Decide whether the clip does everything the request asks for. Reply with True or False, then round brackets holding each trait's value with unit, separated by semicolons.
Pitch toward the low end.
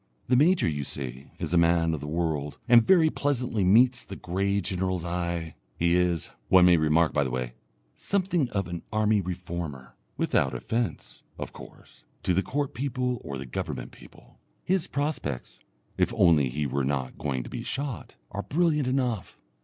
True (90 Hz)